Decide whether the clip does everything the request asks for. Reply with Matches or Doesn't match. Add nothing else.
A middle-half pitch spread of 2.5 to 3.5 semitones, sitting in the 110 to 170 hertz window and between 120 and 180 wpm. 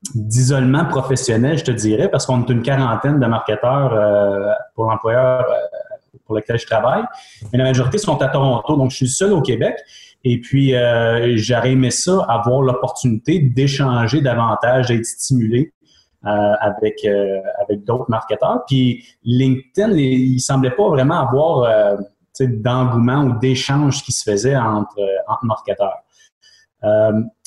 Matches